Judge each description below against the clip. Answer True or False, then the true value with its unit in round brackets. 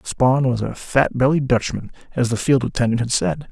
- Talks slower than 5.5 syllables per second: True (5.0 syllables/s)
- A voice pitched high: False (125 Hz)